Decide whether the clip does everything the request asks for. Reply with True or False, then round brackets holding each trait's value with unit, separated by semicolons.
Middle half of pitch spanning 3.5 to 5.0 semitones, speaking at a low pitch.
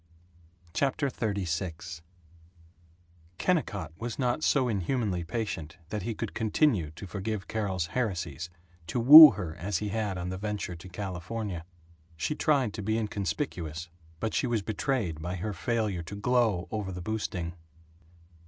True (4.5 semitones; 100 Hz)